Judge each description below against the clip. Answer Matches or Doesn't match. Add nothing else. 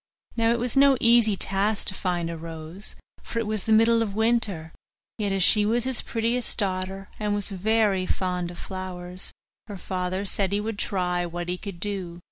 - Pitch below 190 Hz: Doesn't match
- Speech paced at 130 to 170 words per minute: Doesn't match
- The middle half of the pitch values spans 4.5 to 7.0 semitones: Doesn't match